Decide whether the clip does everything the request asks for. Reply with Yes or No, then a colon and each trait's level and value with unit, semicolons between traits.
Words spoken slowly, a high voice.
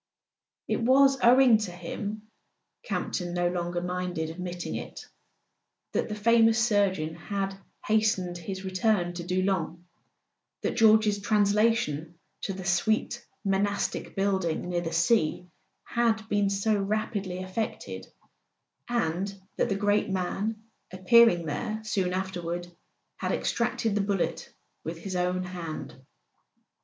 Yes: slow, 120 wpm; high, 195 Hz